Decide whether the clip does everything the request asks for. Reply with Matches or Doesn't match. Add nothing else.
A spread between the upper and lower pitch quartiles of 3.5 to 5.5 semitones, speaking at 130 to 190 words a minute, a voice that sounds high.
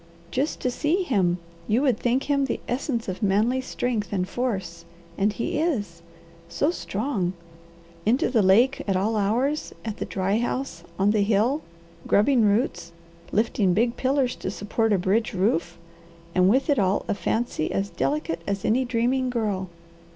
Matches